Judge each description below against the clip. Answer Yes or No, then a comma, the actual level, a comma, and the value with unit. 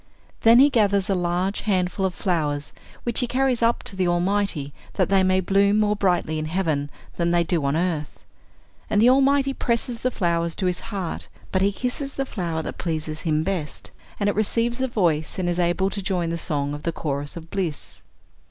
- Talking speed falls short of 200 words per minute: No, fast, 205 wpm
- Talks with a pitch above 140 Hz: Yes, medium, 185 Hz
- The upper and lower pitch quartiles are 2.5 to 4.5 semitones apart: Yes, average, 4.0 semitones